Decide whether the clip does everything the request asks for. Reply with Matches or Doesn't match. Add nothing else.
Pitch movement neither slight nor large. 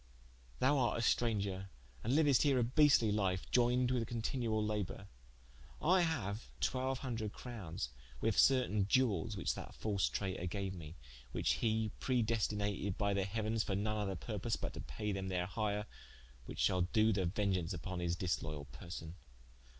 Matches